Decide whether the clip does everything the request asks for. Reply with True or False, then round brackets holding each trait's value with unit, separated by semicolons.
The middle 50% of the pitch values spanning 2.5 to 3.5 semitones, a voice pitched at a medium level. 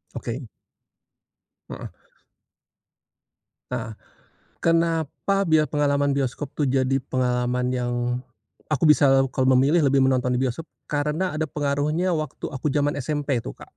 True (2.9 semitones; 145 Hz)